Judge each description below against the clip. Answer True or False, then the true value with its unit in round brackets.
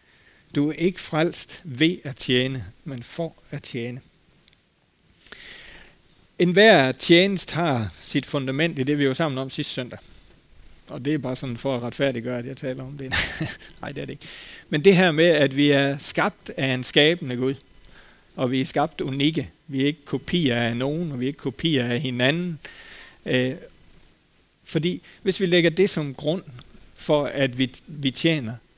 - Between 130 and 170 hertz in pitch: True (140 Hz)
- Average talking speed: True (175 wpm)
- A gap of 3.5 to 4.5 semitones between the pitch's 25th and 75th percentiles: True (4.0 semitones)